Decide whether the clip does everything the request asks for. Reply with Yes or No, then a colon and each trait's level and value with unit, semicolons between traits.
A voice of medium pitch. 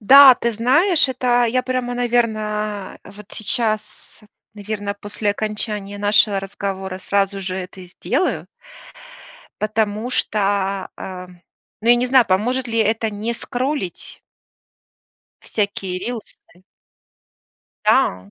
No: high, 215 Hz